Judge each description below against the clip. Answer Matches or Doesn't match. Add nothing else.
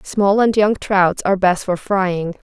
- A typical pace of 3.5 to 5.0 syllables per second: Matches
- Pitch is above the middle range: Matches